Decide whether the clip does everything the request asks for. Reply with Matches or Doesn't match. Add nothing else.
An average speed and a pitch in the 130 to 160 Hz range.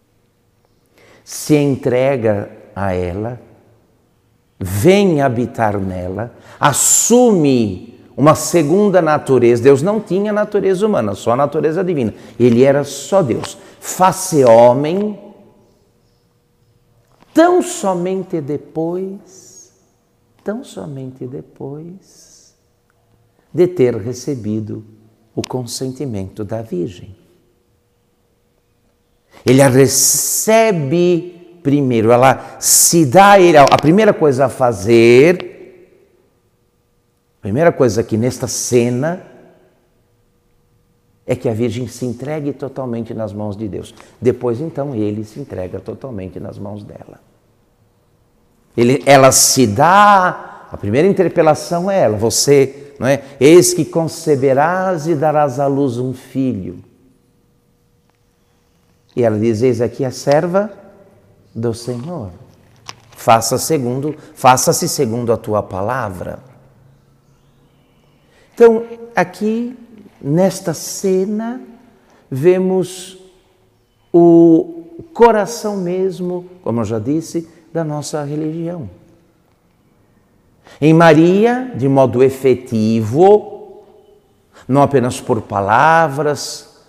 Doesn't match